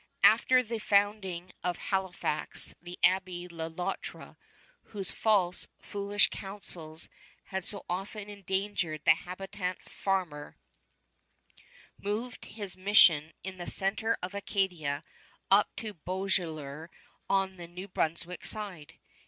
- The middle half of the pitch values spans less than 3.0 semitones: Yes, narrow, 2.6 semitones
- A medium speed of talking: No, slow, 115 wpm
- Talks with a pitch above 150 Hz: Yes, high, 190 Hz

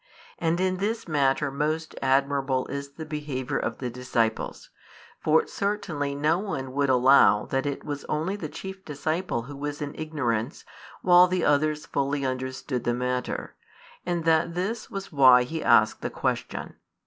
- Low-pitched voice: No, medium, 145 Hz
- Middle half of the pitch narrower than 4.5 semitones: Yes, average, 3.7 semitones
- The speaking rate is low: No, average, 160 wpm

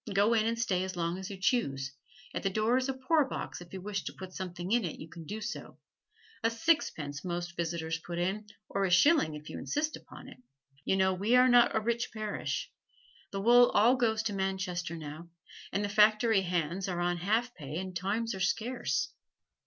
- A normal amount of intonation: Yes, average, 4.7 semitones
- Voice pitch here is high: Yes, high, 195 Hz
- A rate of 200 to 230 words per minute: Yes, fast, 205 wpm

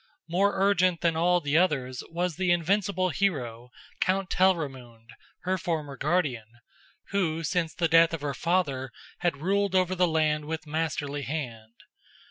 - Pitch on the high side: No, medium, 165 Hz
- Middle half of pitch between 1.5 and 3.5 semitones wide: No, average, 4.3 semitones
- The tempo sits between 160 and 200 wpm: No, average, 145 wpm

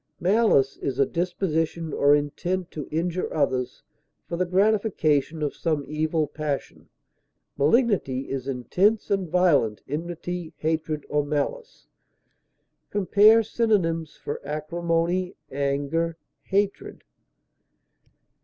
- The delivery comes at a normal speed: No, slow, 100 wpm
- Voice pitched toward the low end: No, medium, 165 Hz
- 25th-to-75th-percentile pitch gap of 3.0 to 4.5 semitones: Yes, average, 4.1 semitones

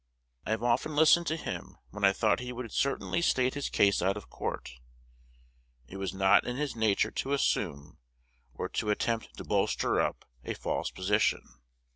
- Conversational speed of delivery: Yes, average, 175 wpm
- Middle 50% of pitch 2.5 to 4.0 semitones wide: No, average, 5.2 semitones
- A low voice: Yes, low, 110 Hz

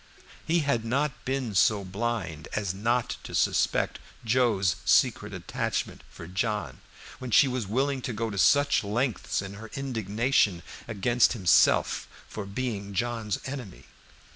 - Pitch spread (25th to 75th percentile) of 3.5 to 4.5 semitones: Yes, average, 4.2 semitones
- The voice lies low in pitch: Yes, low, 115 Hz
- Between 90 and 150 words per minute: Yes, average, 140 wpm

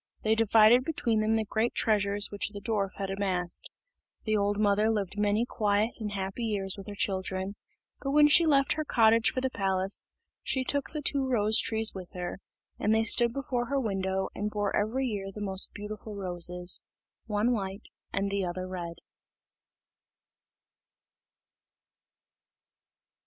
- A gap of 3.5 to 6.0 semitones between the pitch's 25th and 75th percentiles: No, average, 2.8 semitones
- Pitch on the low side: No, high, 210 Hz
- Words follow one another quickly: No, average, 155 wpm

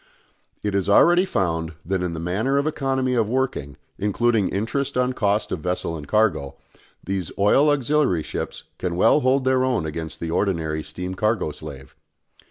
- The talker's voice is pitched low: Yes, low, 100 Hz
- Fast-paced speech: No, average, 170 wpm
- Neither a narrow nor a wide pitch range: No, wide, 7.5 semitones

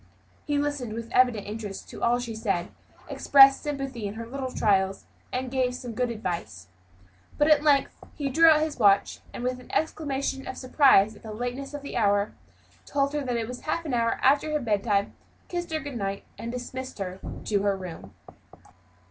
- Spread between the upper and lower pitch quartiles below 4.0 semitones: No, average, 4.8 semitones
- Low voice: No, high, 245 Hz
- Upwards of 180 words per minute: Yes, average, 190 wpm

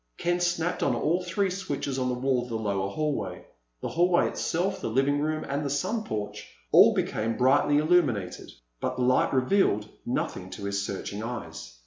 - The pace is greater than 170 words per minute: Yes, average, 180 wpm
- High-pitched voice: No, low, 135 Hz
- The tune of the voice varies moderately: No, wide, 7.0 semitones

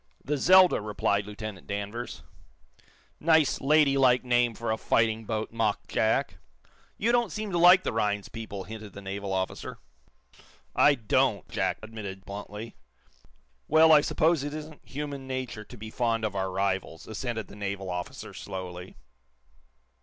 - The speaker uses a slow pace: No, average, 150 wpm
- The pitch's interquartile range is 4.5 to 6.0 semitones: Yes, wide, 5.6 semitones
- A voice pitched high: No, low, 110 Hz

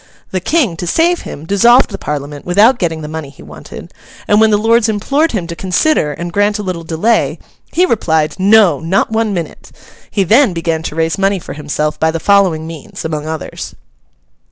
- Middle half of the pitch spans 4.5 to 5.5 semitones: Yes, average, 5.1 semitones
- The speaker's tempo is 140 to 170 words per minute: No, average, 195 wpm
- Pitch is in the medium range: Yes, medium, 180 Hz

